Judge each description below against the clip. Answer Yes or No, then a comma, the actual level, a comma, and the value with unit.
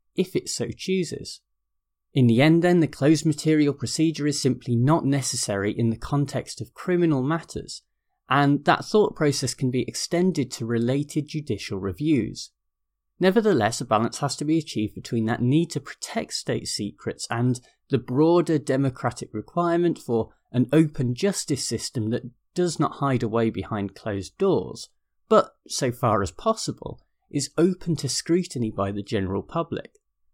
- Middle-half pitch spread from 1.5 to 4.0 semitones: No, wide, 5.5 semitones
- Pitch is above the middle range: No, low, 135 Hz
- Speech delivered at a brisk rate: No, average, 155 wpm